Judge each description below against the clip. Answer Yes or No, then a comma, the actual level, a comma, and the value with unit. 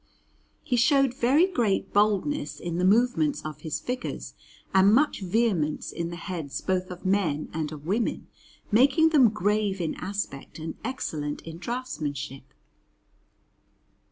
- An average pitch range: No, wide, 7.0 semitones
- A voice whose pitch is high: Yes, high, 195 Hz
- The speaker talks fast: No, slow, 135 wpm